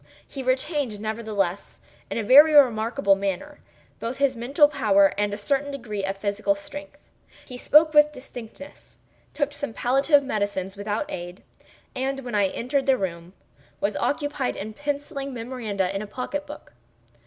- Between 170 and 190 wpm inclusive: No, average, 145 wpm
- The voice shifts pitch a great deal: Yes, wide, 5.7 semitones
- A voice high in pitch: Yes, high, 245 Hz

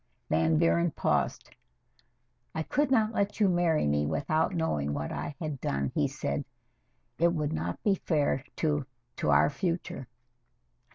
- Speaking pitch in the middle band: Yes, medium, 150 Hz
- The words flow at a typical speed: Yes, average, 150 wpm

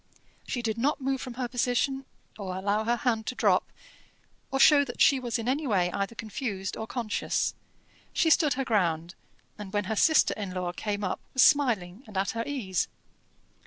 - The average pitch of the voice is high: Yes, high, 230 Hz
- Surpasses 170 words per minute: Yes, average, 190 wpm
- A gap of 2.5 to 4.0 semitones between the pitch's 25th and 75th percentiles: No, average, 4.8 semitones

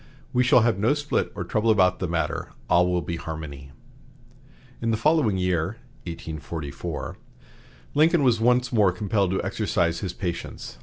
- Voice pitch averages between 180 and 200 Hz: No, very low, 95 Hz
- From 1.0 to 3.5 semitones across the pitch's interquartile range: No, average, 5.3 semitones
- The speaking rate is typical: Yes, average, 155 wpm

